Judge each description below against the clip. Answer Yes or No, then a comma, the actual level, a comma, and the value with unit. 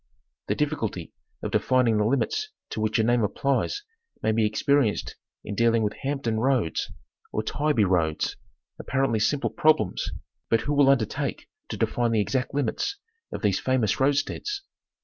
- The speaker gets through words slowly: No, average, 155 wpm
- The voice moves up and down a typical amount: Yes, average, 4.5 semitones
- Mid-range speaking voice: No, low, 120 Hz